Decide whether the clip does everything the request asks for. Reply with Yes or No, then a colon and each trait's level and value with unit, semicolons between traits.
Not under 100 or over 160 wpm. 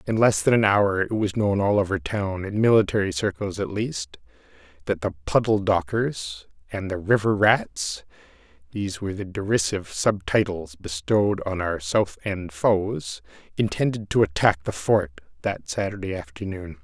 Yes: average, 155 wpm